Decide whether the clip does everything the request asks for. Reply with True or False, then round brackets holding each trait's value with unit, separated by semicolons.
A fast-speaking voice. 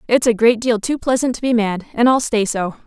True (270 wpm)